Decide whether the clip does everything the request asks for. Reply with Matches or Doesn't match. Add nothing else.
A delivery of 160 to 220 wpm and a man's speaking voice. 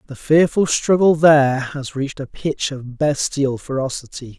Doesn't match